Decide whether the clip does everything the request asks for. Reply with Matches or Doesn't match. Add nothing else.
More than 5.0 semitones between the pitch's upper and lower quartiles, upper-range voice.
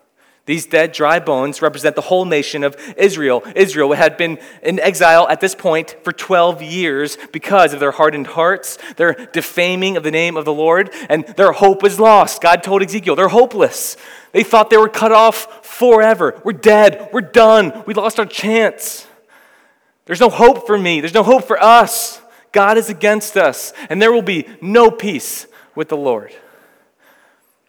Matches